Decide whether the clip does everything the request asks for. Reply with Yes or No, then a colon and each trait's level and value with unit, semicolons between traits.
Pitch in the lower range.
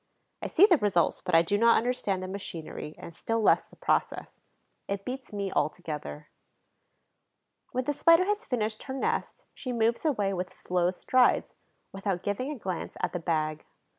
No: high, 205 Hz